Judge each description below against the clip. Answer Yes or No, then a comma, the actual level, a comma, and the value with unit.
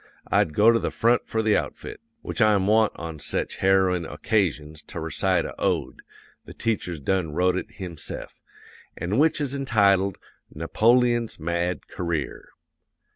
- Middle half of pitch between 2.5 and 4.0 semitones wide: No, average, 4.8 semitones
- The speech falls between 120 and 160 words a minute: Yes, average, 145 wpm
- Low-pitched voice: Yes, very low, 95 Hz